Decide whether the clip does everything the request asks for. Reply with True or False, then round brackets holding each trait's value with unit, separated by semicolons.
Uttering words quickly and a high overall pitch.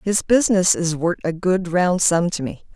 False (220 wpm; 180 Hz)